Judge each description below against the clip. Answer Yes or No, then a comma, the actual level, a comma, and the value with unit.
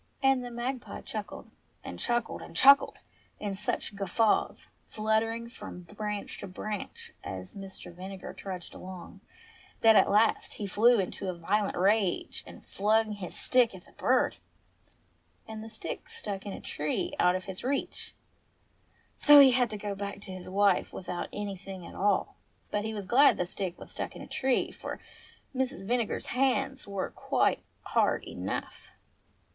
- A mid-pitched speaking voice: No, high, 205 Hz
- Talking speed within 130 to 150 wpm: No, average, 165 wpm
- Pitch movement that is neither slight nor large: Yes, average, 3.5 semitones